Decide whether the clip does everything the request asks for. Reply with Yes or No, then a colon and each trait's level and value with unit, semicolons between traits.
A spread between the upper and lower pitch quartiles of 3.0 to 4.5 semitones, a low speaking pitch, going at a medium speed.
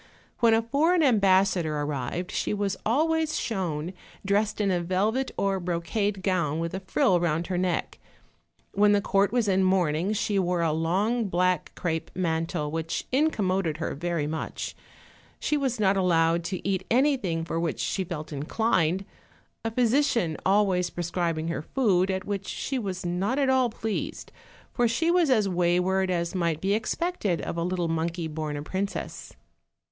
No: average, 4.1 semitones; medium, 185 Hz; average, 165 wpm